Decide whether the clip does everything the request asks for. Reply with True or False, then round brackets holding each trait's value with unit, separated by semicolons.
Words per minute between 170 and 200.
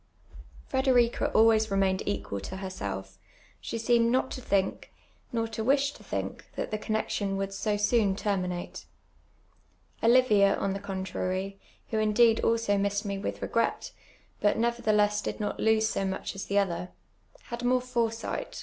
False (150 wpm)